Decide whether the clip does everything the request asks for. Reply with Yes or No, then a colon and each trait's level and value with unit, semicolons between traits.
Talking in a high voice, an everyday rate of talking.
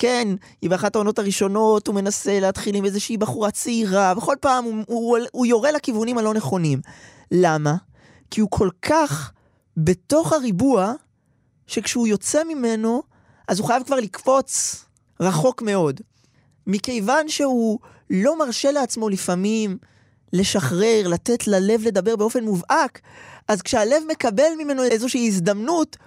Yes: high, 220 Hz; average, 130 wpm